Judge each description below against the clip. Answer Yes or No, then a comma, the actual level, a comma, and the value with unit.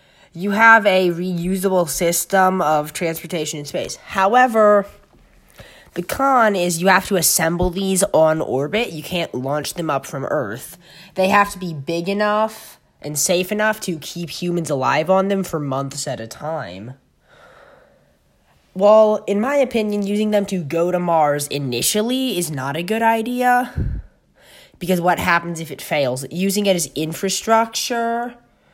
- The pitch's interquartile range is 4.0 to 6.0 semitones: Yes, average, 4.7 semitones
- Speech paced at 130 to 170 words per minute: Yes, average, 150 wpm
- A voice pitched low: No, medium, 185 Hz